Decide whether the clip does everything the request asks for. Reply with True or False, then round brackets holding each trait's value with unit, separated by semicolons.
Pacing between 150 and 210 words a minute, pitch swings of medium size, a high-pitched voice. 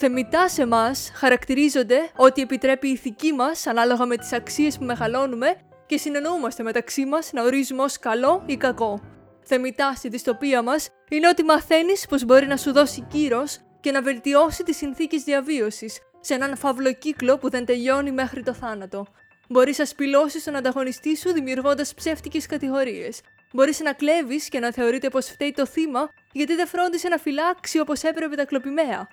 True (170 wpm; 3.0 semitones; 275 Hz)